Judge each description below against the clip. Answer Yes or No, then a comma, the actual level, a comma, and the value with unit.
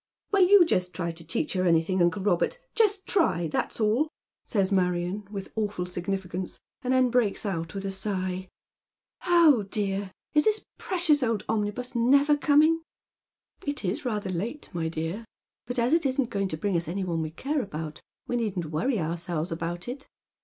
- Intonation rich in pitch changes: Yes, wide, 6.7 semitones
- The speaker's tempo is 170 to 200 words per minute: Yes, average, 195 wpm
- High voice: Yes, high, 200 Hz